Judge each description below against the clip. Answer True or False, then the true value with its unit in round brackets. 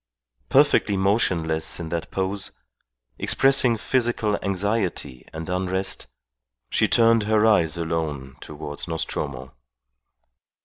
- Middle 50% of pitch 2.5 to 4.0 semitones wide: False (5.2 semitones)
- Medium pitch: False (95 Hz)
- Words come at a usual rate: False (95 wpm)